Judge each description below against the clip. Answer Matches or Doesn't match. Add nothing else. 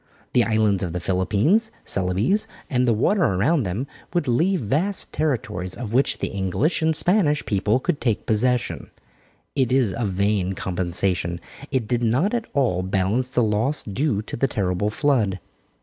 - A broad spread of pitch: Matches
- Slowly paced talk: Doesn't match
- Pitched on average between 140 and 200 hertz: Doesn't match